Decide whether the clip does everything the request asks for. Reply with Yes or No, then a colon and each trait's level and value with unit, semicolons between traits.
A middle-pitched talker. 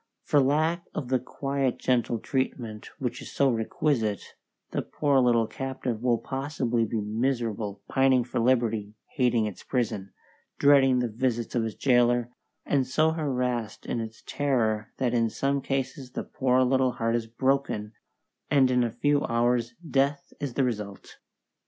No: low, 125 Hz